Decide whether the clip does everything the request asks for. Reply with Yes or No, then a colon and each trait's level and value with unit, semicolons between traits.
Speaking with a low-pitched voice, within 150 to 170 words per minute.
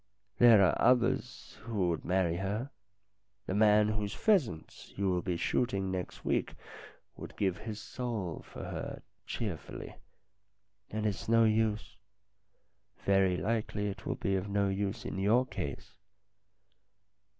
No: low, 100 Hz; slow, 135 wpm